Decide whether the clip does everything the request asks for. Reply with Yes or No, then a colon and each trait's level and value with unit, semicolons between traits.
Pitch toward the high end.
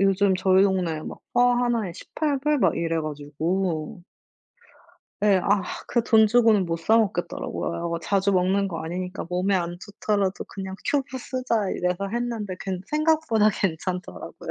Yes: high, 195 Hz